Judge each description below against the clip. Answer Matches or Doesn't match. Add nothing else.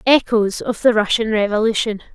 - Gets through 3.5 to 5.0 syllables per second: Doesn't match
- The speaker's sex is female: Matches